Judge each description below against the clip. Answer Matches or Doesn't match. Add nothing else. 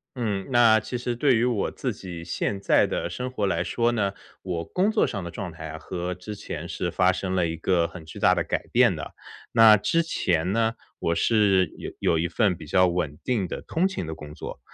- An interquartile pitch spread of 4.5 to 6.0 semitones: Matches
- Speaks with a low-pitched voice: Matches